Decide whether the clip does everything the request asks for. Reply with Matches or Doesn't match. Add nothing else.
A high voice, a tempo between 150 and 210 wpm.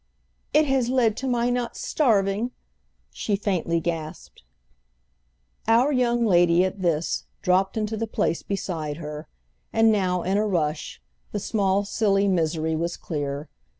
Doesn't match